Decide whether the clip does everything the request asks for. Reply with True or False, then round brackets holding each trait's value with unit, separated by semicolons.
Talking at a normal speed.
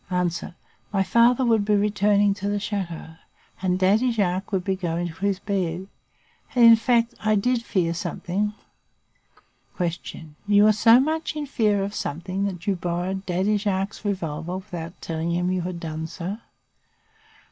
True (160 wpm)